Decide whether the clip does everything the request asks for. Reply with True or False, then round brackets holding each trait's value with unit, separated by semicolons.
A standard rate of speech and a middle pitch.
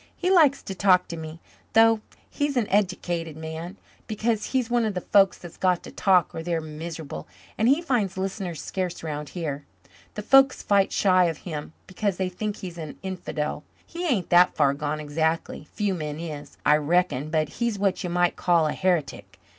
True (190 wpm; 180 Hz)